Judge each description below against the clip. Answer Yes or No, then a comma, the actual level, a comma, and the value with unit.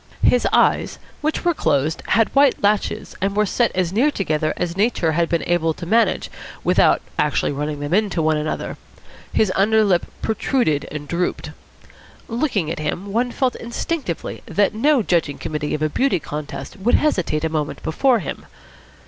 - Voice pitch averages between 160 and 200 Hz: Yes, medium, 185 Hz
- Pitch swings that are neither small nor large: No, wide, 6.6 semitones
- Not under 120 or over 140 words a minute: No, average, 170 wpm